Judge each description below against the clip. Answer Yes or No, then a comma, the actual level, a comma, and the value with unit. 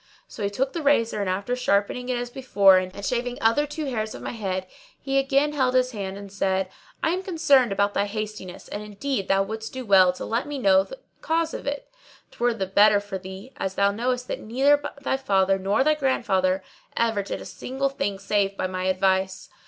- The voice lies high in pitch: Yes, high, 215 Hz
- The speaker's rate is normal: No, fast, 215 wpm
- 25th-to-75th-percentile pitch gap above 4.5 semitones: Yes, average, 5.2 semitones